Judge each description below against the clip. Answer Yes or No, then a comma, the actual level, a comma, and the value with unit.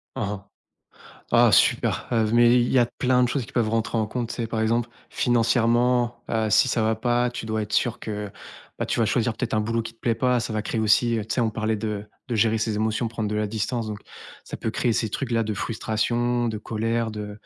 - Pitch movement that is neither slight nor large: No, narrow, 1.7 semitones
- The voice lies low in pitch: Yes, low, 115 Hz